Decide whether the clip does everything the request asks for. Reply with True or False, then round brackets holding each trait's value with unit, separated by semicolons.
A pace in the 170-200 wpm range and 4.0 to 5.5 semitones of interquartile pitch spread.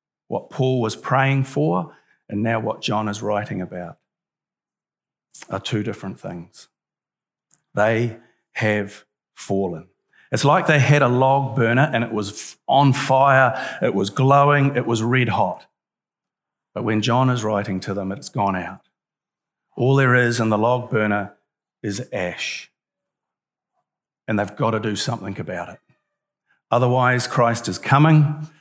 False (145 wpm; 4.3 semitones)